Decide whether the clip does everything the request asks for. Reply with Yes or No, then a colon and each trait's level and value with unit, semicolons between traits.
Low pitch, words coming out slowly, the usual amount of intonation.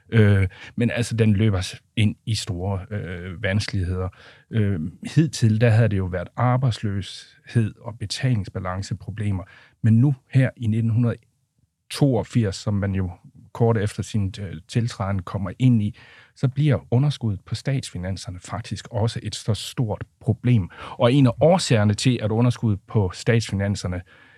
Yes: low, 110 Hz; slow, 135 wpm; average, 3.4 semitones